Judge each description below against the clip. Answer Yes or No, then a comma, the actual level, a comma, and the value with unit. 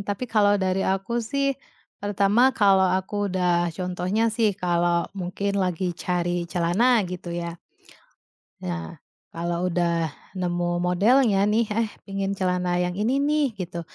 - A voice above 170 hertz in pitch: Yes, high, 190 Hz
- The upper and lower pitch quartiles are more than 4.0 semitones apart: No, average, 2.9 semitones